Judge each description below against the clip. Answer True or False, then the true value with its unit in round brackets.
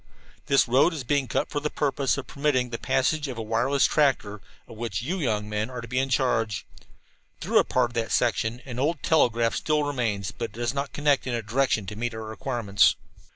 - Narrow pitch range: False (3.6 semitones)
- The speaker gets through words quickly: True (220 wpm)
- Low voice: True (125 Hz)